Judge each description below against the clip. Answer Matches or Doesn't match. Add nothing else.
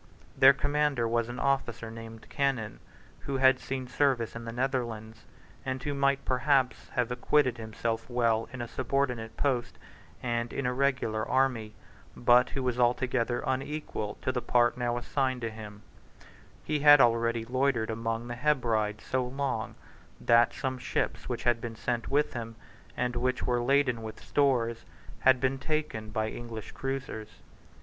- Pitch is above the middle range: Doesn't match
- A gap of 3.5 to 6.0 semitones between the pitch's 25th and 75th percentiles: Doesn't match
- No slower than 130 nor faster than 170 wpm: Matches